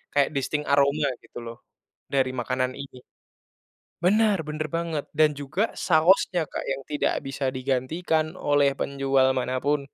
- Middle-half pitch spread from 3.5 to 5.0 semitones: No, average, 2.8 semitones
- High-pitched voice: No, medium, 140 Hz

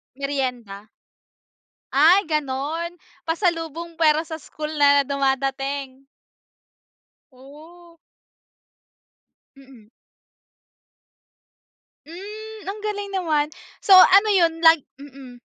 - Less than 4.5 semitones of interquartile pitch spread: Yes, average, 4.0 semitones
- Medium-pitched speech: No, very high, 305 Hz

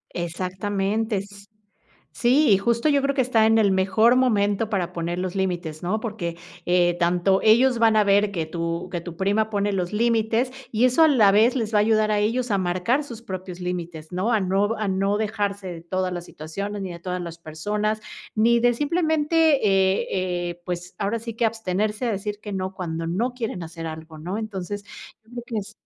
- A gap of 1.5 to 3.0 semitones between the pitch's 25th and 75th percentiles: No, average, 3.8 semitones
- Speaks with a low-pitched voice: No, high, 200 Hz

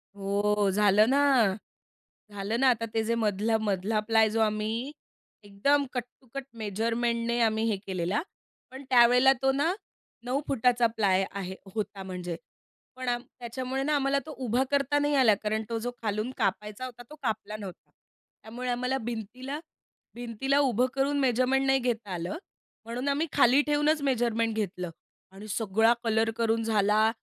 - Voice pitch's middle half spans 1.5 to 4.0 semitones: Yes, average, 3.7 semitones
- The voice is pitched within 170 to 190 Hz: No, high, 230 Hz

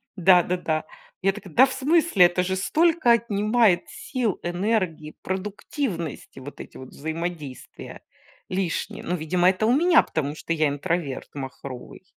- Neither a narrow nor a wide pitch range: No, wide, 5.9 semitones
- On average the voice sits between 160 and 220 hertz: Yes, medium, 185 Hz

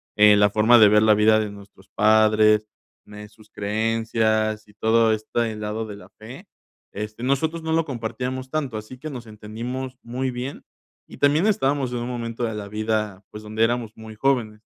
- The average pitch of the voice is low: Yes, low, 110 Hz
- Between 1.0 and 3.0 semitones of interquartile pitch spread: Yes, average, 2.7 semitones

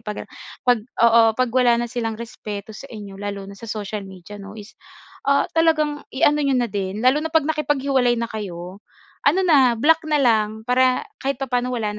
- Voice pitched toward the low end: No, high, 240 Hz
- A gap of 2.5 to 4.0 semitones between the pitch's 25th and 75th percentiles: No, average, 4.6 semitones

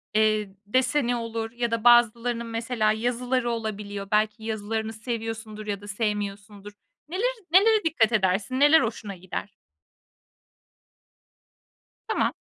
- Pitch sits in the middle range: No, high, 225 Hz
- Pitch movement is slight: Yes, narrow, 2.3 semitones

